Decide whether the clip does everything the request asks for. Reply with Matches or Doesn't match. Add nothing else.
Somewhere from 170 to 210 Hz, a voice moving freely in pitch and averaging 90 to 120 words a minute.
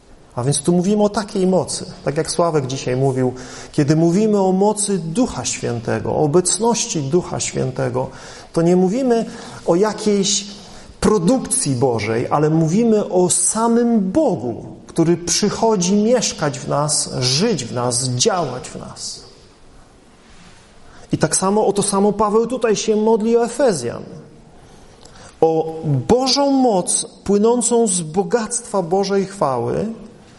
Doesn't match